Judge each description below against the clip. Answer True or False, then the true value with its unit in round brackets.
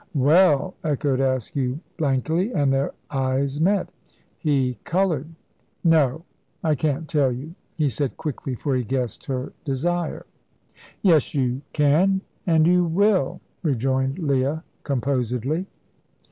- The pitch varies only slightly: False (3.7 semitones)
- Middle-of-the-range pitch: True (145 Hz)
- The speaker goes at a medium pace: False (120 wpm)